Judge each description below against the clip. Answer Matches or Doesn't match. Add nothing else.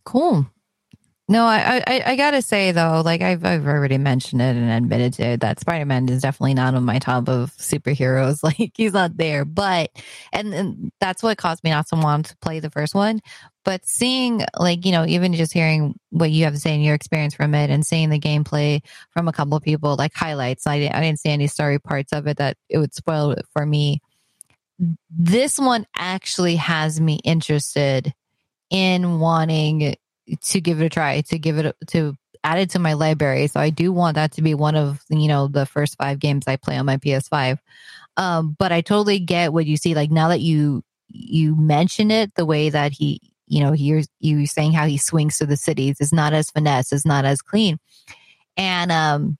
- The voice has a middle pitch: Matches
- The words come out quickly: Matches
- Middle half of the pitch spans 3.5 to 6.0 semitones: Doesn't match